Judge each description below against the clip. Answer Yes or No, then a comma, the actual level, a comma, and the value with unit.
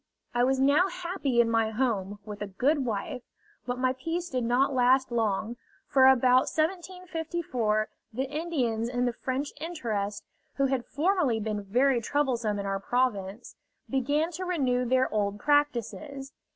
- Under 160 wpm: Yes, average, 150 wpm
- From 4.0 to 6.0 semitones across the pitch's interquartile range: Yes, average, 4.3 semitones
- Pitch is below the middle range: No, very high, 255 Hz